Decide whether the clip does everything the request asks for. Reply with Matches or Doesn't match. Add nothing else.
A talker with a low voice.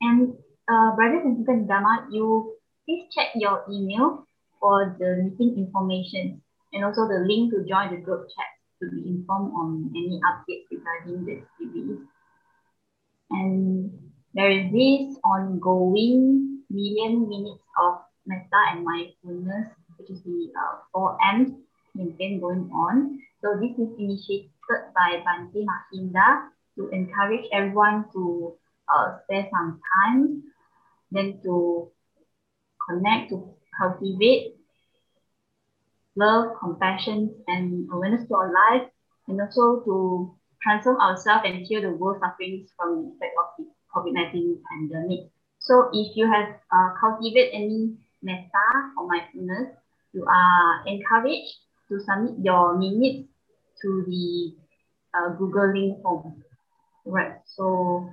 Doesn't match